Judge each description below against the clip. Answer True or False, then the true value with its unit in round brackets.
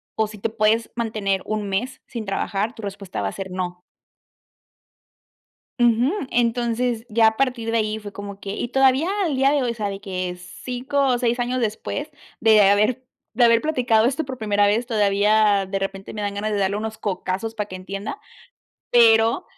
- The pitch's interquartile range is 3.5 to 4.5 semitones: False (3.1 semitones)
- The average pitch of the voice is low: False (220 Hz)